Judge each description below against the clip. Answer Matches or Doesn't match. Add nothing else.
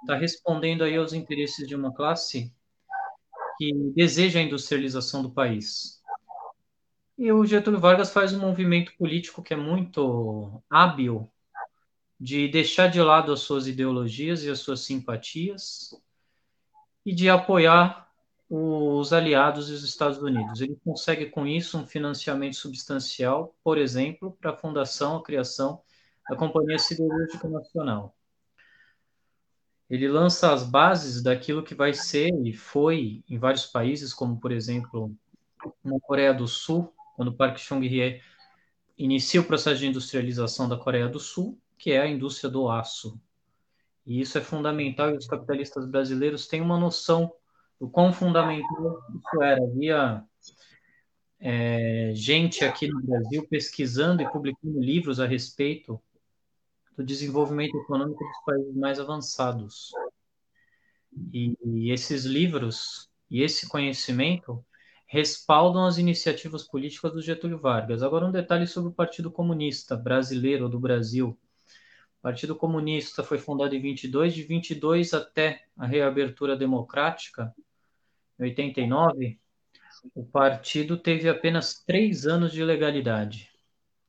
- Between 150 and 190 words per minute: Doesn't match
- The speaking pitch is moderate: Matches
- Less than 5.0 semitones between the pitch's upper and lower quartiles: Matches